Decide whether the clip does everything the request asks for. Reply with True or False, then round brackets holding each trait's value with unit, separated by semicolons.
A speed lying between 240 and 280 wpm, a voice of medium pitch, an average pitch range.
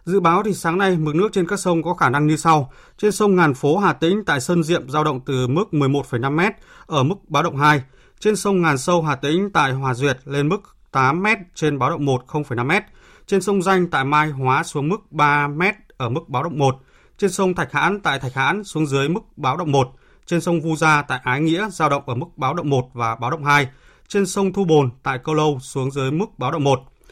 True (250 wpm; 155 Hz; 5.0 semitones)